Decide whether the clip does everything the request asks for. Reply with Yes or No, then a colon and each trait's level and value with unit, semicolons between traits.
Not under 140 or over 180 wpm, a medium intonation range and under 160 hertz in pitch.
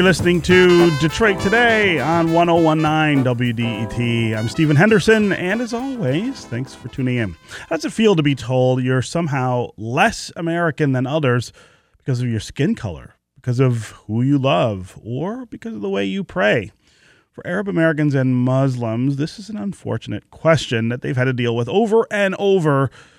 No: average, 175 wpm; wide, 6.4 semitones; medium, 140 Hz